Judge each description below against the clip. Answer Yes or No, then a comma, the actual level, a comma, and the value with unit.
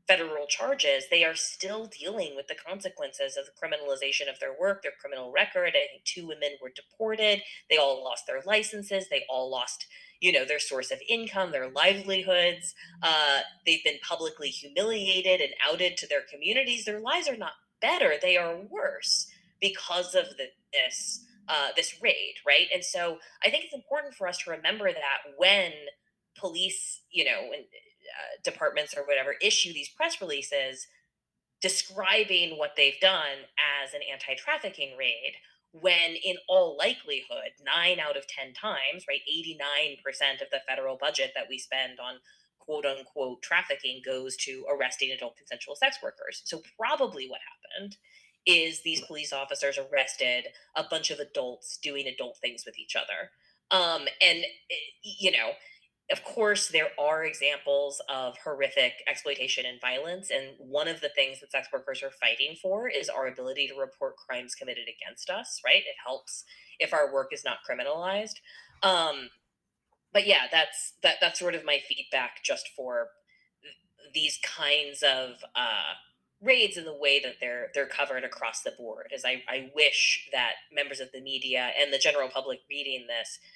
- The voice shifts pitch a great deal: Yes, wide, 7.8 semitones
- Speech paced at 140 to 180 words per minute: Yes, average, 165 wpm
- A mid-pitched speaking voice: Yes, medium, 180 Hz